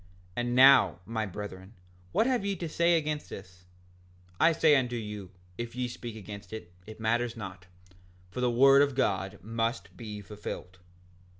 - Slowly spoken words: No, average, 165 wpm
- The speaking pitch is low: Yes, low, 115 Hz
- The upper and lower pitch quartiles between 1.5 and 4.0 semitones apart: No, average, 4.7 semitones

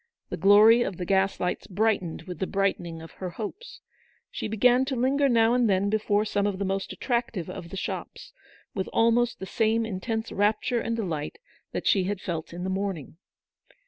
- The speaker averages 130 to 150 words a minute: No, average, 190 wpm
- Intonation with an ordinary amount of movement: Yes, average, 3.4 semitones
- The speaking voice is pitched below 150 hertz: No, high, 205 Hz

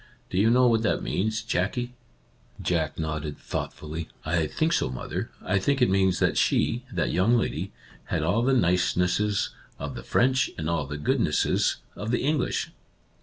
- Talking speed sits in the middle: Yes, average, 185 wpm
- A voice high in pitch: No, very low, 95 Hz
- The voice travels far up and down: Yes, wide, 6.7 semitones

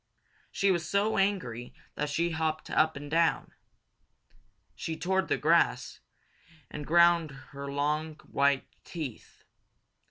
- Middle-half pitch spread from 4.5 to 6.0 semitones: No, average, 3.1 semitones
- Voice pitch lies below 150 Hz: No, medium, 160 Hz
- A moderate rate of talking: No, slow, 125 wpm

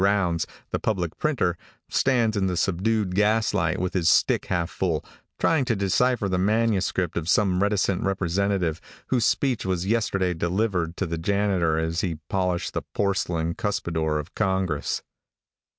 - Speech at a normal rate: Yes, average, 150 wpm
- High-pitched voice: No, very low, 95 Hz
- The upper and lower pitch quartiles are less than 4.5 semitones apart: Yes, average, 3.2 semitones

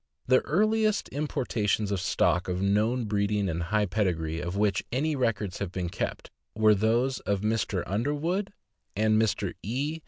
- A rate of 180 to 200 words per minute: No, average, 155 wpm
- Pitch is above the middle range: No, low, 105 Hz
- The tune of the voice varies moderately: Yes, average, 4.8 semitones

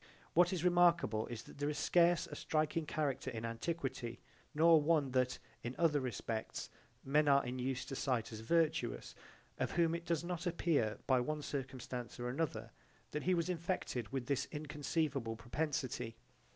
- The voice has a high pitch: No, medium, 145 Hz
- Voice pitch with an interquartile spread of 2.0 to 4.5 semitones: No, average, 4.9 semitones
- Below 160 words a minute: No, average, 165 wpm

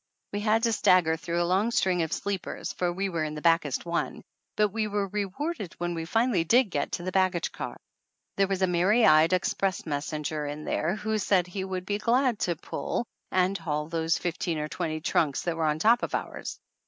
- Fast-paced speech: Yes, fast, 215 wpm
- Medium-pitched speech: Yes, medium, 180 Hz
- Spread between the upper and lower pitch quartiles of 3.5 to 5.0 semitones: Yes, average, 3.9 semitones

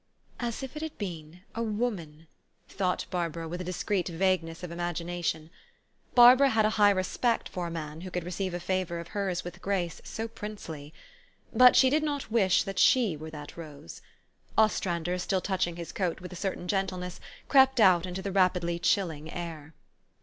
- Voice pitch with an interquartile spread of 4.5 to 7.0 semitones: No, average, 3.5 semitones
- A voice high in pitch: No, medium, 180 Hz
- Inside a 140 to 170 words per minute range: No, average, 180 wpm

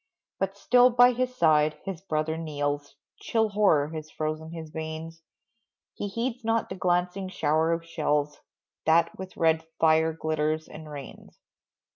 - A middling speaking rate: Yes, average, 145 wpm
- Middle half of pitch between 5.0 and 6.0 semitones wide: No, average, 3.8 semitones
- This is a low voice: No, medium, 160 Hz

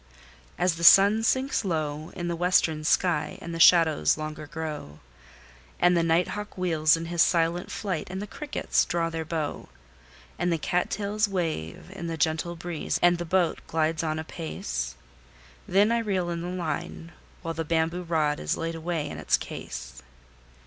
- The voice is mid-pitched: Yes, medium, 165 Hz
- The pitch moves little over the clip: Yes, narrow, 2.2 semitones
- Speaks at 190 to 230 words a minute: No, average, 175 wpm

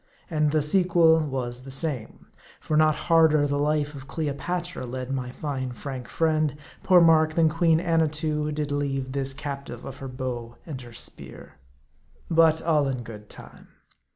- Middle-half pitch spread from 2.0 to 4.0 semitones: Yes, average, 3.4 semitones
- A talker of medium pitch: Yes, medium, 150 Hz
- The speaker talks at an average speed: Yes, average, 155 wpm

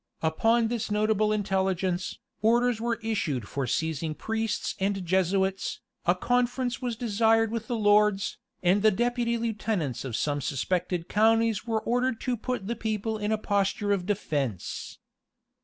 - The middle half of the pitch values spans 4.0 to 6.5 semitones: No, average, 3.4 semitones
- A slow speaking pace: No, average, 145 wpm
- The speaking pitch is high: Yes, high, 210 Hz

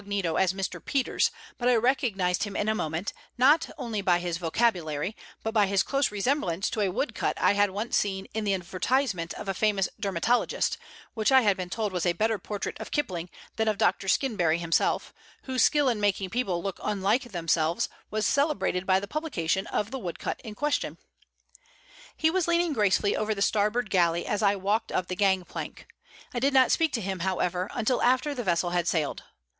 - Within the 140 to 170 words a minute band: No, average, 200 wpm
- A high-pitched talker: Yes, high, 205 Hz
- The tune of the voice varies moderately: Yes, average, 4.9 semitones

